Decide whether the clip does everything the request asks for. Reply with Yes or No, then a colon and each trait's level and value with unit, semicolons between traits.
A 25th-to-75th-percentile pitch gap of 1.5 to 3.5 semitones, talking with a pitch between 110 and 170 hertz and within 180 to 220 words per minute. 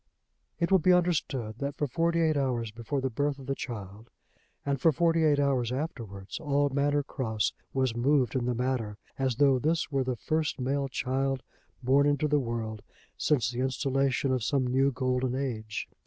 Yes: average, 2.9 semitones; low, 135 Hz; average, 185 wpm